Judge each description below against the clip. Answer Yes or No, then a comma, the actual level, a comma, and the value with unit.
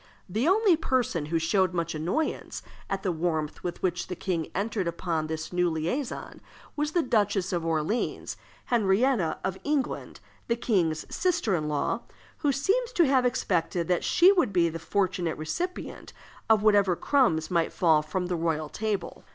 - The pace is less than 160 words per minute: No, average, 165 wpm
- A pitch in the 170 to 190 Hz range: Yes, medium, 185 Hz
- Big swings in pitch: Yes, wide, 6.9 semitones